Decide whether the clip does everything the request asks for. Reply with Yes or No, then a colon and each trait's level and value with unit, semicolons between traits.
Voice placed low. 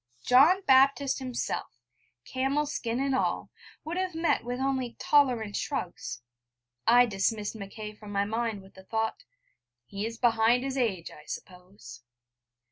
No: high, 235 Hz